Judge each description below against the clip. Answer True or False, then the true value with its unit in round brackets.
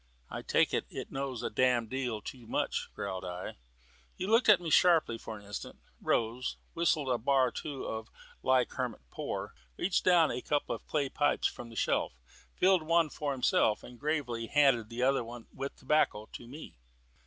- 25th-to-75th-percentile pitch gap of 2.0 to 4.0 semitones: False (4.6 semitones)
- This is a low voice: True (130 Hz)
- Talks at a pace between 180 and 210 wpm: True (190 wpm)